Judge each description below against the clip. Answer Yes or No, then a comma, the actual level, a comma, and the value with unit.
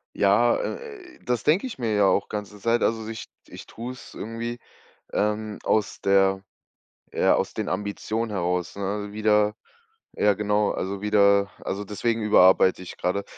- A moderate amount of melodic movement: No, narrow, 2.3 semitones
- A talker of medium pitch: No, low, 105 Hz